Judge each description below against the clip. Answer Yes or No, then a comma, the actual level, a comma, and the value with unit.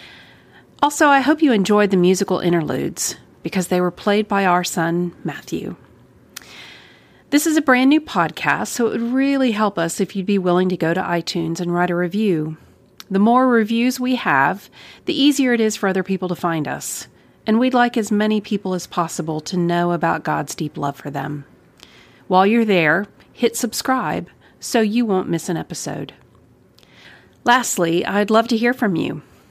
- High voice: Yes, high, 195 Hz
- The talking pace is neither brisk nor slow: Yes, average, 180 wpm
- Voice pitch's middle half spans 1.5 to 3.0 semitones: No, average, 5.3 semitones